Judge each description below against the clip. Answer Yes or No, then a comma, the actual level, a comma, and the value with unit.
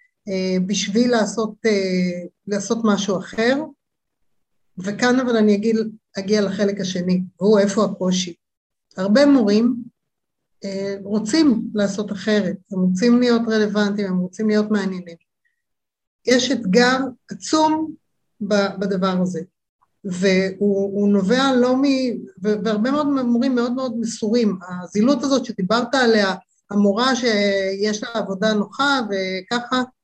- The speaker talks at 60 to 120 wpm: Yes, average, 115 wpm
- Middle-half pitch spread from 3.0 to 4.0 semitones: Yes, average, 3.7 semitones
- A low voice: No, high, 210 Hz